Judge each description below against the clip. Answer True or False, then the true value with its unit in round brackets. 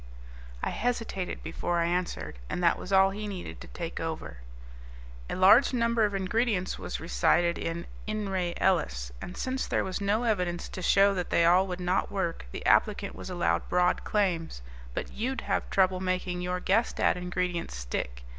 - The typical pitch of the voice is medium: True (180 Hz)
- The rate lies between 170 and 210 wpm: True (180 wpm)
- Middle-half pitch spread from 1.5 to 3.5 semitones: True (2.6 semitones)